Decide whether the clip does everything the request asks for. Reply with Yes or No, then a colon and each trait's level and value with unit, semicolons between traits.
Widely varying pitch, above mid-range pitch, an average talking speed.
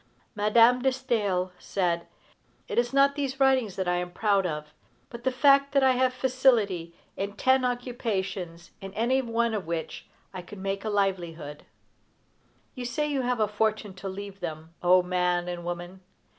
Yes: wide, 5.8 semitones; high, 205 Hz; average, 170 wpm